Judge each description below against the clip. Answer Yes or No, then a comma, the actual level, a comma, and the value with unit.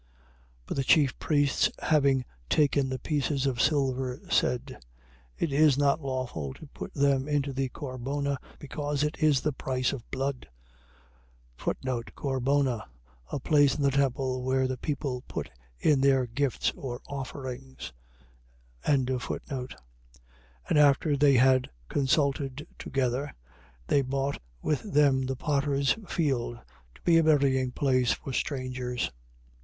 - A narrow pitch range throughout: Yes, narrow, 1.8 semitones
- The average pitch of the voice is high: No, low, 135 Hz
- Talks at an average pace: No, slow, 130 wpm